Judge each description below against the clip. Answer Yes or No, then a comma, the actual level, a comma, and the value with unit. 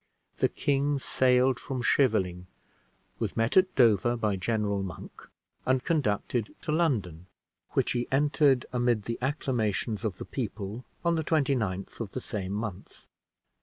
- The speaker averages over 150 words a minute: No, average, 140 wpm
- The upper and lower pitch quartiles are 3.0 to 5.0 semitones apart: Yes, average, 4.7 semitones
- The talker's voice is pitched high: No, low, 120 Hz